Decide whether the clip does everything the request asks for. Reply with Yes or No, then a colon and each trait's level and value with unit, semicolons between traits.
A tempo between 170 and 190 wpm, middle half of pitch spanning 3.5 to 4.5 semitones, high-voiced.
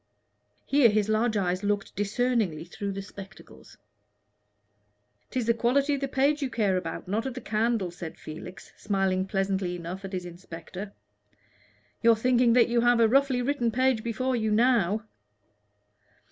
No: average, 155 wpm; average, 4.2 semitones; high, 215 Hz